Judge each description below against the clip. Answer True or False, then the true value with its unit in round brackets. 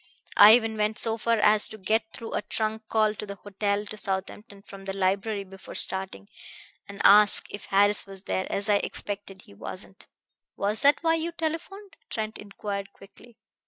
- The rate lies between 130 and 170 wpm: False (180 wpm)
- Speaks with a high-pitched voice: True (210 Hz)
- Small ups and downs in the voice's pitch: True (1.9 semitones)